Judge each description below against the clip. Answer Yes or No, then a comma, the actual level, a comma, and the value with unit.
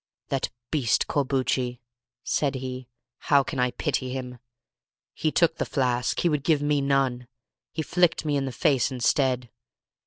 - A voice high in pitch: No, low, 135 Hz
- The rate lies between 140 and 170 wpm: Yes, average, 150 wpm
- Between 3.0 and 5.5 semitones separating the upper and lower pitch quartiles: No, narrow, 2.6 semitones